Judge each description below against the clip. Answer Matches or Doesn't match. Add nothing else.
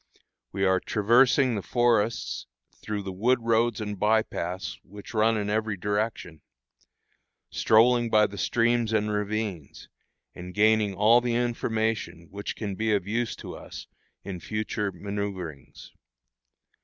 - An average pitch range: Doesn't match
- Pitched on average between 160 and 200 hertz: Doesn't match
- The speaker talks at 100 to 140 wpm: Matches